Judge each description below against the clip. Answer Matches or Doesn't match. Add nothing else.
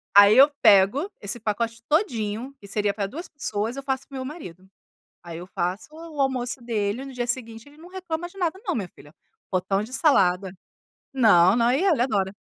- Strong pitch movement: Matches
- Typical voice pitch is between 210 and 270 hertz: Matches